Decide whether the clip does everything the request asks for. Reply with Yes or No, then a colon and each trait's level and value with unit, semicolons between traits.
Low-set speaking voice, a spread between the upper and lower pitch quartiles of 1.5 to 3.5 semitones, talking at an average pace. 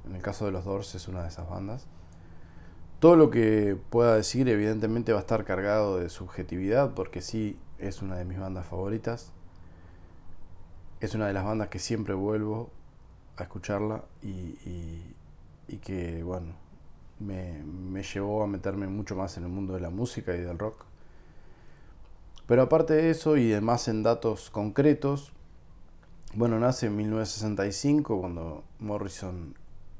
No: very low, 95 Hz; average, 3.9 semitones; average, 155 wpm